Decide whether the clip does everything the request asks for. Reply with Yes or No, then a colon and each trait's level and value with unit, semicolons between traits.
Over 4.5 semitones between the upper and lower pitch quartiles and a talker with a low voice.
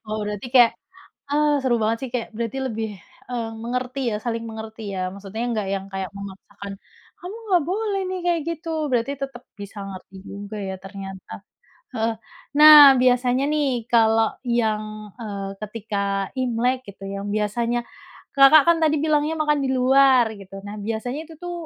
No: average, 4.9 semitones; high, 235 Hz